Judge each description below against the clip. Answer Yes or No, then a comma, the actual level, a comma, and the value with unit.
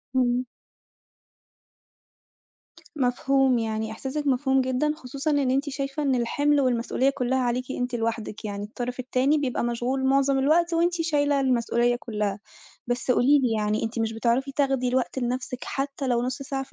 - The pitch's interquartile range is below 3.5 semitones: Yes, narrow, 2.4 semitones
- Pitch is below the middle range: No, very high, 255 Hz